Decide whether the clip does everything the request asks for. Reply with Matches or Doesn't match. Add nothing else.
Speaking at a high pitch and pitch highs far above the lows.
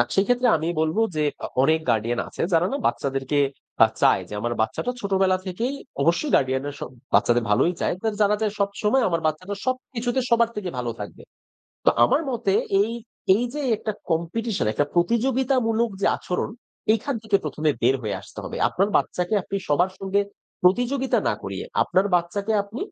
Matches